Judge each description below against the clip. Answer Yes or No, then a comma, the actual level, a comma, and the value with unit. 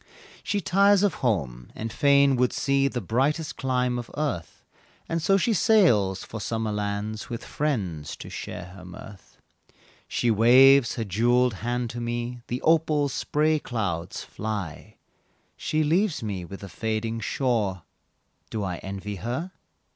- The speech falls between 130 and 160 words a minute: Yes, average, 145 wpm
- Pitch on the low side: Yes, low, 120 Hz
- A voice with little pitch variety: No, wide, 5.4 semitones